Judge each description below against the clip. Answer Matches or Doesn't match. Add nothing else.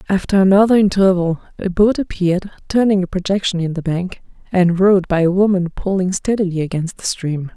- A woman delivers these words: Matches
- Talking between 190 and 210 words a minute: Doesn't match